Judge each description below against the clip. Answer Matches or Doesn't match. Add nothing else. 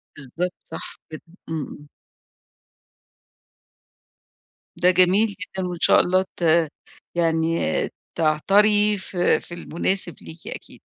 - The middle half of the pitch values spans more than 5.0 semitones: Doesn't match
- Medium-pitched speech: Matches